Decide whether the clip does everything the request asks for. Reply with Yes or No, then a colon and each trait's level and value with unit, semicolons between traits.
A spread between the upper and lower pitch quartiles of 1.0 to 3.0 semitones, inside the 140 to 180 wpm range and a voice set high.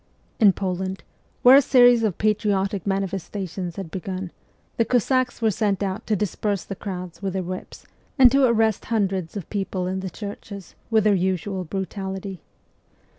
Yes: narrow, 2.4 semitones; average, 160 wpm; high, 195 Hz